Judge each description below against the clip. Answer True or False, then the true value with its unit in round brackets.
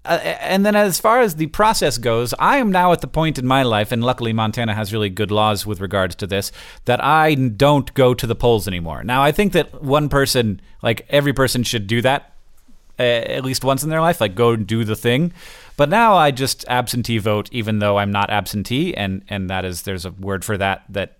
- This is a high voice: False (120 Hz)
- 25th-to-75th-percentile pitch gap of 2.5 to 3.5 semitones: False (5.6 semitones)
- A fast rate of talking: True (230 wpm)